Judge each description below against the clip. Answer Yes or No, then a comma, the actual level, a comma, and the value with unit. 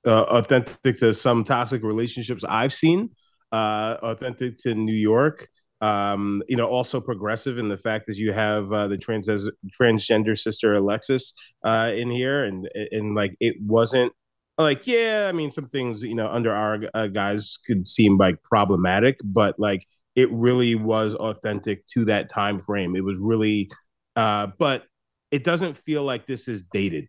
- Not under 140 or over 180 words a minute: Yes, average, 170 wpm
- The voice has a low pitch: Yes, low, 110 Hz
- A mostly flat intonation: No, average, 3.0 semitones